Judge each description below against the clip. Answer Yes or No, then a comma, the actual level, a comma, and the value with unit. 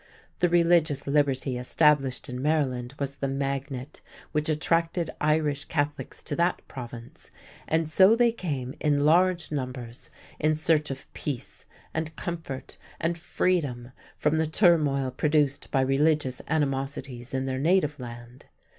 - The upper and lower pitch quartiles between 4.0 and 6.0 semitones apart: No, average, 3.2 semitones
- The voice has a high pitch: No, medium, 145 Hz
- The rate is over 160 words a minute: No, slow, 135 wpm